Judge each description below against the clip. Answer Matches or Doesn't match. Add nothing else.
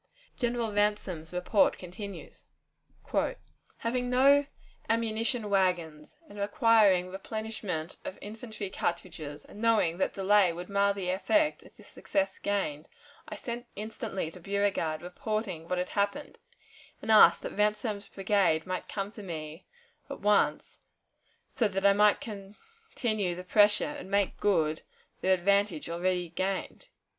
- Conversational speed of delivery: Doesn't match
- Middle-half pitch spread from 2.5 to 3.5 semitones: Matches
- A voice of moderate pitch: Doesn't match